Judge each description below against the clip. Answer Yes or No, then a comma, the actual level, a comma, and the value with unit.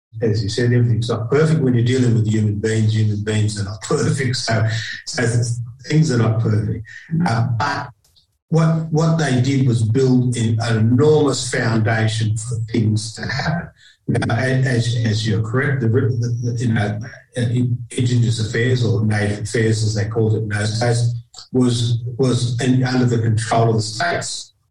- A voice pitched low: Yes, low, 120 Hz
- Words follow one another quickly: No, average, 175 wpm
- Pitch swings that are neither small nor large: No, narrow, 2.3 semitones